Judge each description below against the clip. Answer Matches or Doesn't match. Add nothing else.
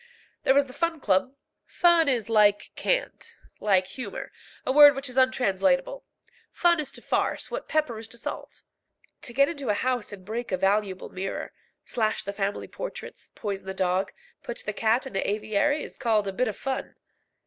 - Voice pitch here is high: Matches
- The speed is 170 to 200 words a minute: Matches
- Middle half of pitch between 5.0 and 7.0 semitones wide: Matches